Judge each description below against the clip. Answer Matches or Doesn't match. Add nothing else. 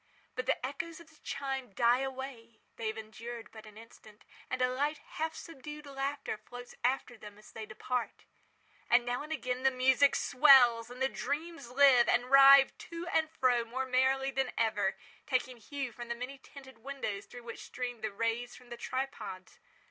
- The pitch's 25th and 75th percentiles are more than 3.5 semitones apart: Doesn't match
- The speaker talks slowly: Doesn't match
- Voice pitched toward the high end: Matches